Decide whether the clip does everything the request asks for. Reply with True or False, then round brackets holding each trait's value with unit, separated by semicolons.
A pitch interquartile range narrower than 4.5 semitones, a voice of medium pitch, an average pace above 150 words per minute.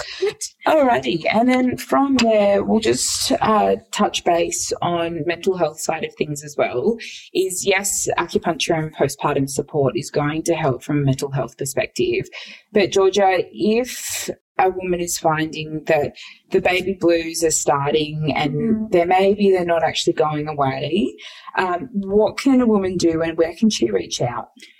False (4.9 semitones; 175 Hz; 160 wpm)